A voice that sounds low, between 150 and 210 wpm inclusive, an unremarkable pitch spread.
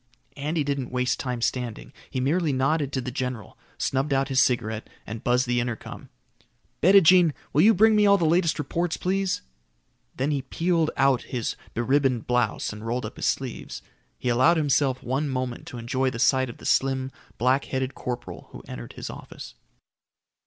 Yes: low, 130 Hz; average, 180 wpm; average, 3.7 semitones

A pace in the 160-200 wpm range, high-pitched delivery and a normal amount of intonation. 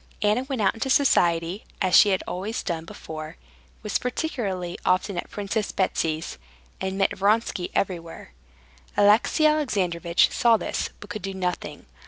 No: average, 140 wpm; high, 195 Hz; average, 3.8 semitones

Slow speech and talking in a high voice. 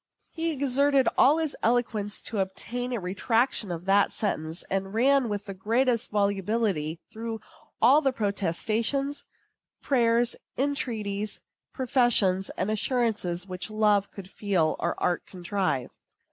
Yes: slow, 125 wpm; high, 215 Hz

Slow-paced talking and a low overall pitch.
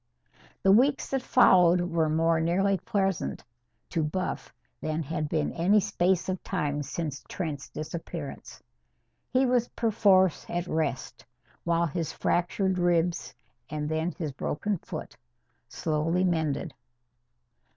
No: slow, 120 wpm; medium, 170 Hz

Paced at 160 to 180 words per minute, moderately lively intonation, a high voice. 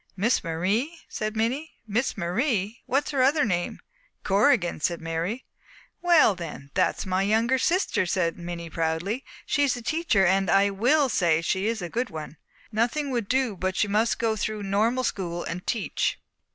No: average, 170 wpm; wide, 5.8 semitones; high, 210 Hz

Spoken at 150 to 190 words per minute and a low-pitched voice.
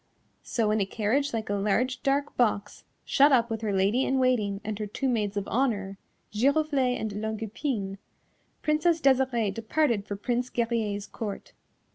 No: average, 165 wpm; high, 225 Hz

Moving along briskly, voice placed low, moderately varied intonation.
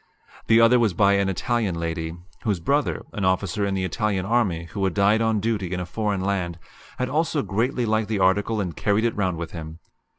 Yes: fast, 210 wpm; low, 100 Hz; average, 3.4 semitones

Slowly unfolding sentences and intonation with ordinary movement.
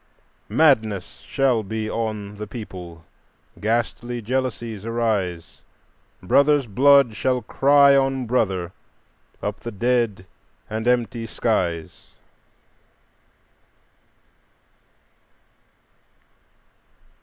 Yes: slow, 75 wpm; average, 3.6 semitones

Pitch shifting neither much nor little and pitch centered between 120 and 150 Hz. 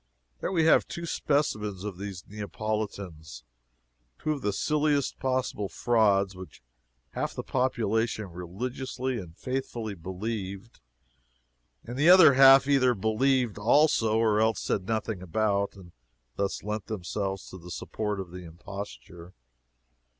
No: average, 4.9 semitones; low, 105 Hz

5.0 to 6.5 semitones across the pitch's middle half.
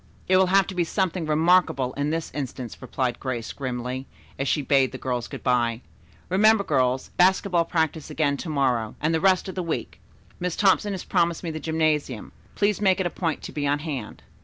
Yes: wide, 5.5 semitones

